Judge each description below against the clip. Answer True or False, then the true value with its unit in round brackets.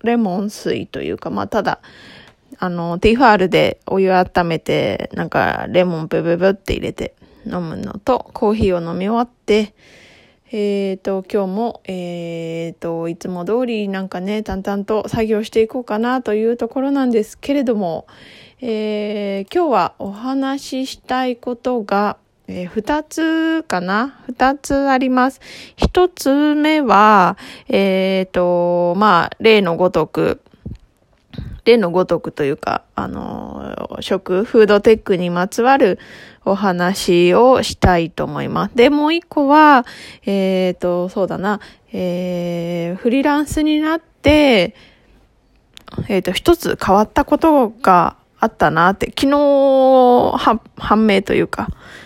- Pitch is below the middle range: False (210 Hz)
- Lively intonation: True (5.9 semitones)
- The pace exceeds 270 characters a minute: False (260 characters per minute)